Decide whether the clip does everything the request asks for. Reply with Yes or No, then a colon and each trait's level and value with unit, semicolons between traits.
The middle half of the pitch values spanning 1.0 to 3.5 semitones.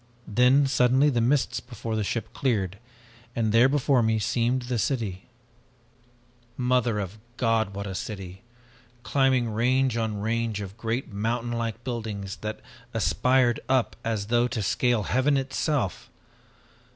Yes: average, 2.9 semitones